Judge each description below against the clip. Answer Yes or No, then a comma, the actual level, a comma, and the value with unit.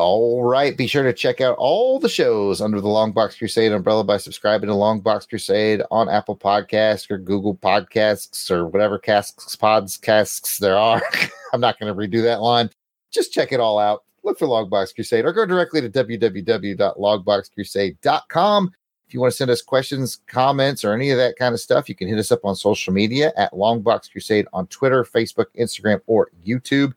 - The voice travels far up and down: No, average, 3.5 semitones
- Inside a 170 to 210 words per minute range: Yes, average, 190 wpm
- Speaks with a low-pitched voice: Yes, low, 110 Hz